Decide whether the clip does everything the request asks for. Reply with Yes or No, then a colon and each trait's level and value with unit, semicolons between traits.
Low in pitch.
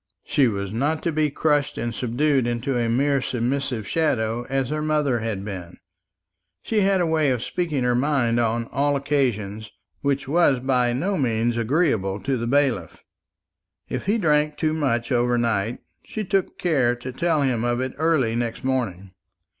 Yes: low, 130 Hz